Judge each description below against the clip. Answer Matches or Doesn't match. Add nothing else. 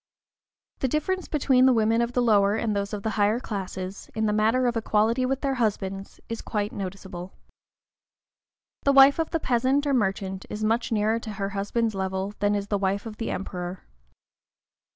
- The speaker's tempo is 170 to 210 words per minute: Matches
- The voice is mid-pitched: Doesn't match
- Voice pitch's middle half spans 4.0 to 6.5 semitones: Doesn't match